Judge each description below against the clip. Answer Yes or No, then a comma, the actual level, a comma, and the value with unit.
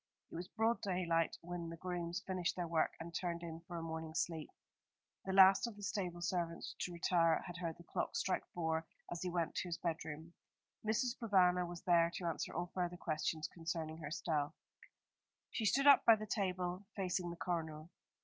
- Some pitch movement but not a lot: No, narrow, 2.0 semitones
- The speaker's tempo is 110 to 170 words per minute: No, average, 190 wpm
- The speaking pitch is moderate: Yes, medium, 175 Hz